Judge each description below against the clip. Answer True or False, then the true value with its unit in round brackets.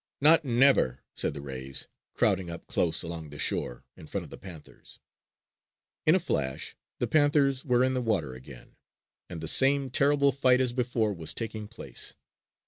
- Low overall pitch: True (115 Hz)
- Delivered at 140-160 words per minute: False (170 wpm)